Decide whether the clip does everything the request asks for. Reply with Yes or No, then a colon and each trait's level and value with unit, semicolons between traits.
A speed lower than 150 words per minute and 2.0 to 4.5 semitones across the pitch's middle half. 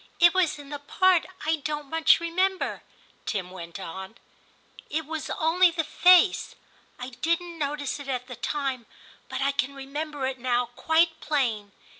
No: average, 170 wpm; average, 4.2 semitones